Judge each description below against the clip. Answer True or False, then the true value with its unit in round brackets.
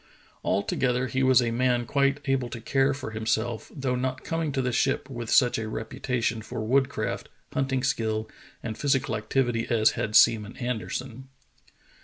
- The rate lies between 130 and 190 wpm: True (160 wpm)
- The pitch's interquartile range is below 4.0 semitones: True (3.0 semitones)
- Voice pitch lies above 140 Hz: False (125 Hz)